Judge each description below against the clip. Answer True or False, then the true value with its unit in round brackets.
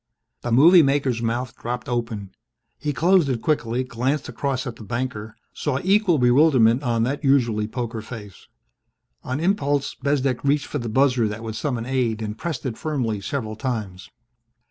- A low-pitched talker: True (125 Hz)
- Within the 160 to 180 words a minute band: True (165 wpm)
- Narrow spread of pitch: False (3.7 semitones)